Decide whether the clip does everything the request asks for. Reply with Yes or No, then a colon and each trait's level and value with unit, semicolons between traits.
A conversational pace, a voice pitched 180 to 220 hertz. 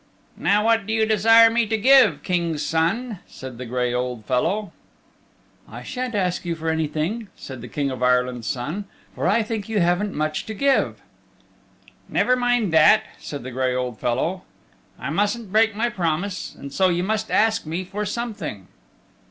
Yes: average, 175 wpm; medium, 185 Hz